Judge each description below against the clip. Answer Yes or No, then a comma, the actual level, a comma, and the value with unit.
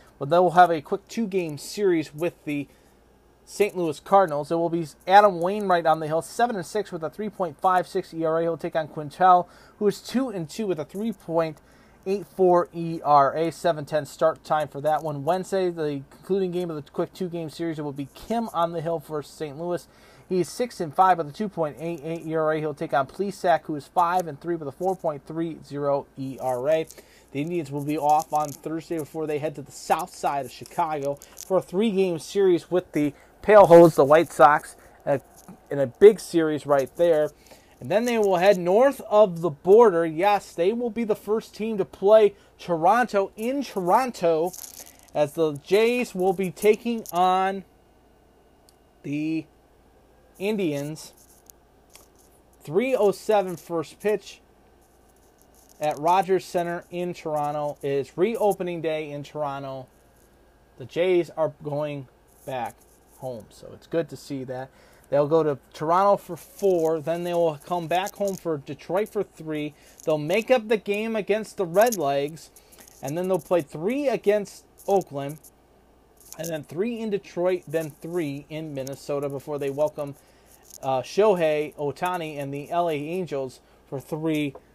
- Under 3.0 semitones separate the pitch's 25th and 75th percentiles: No, average, 4.1 semitones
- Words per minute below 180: Yes, average, 160 wpm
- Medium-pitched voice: Yes, medium, 165 Hz